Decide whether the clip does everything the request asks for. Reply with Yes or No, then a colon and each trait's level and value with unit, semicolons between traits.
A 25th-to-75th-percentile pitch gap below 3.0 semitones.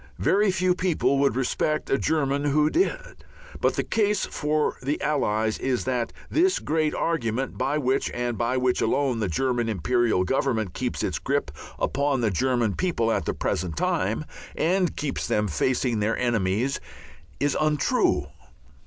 No: average, 4.7 semitones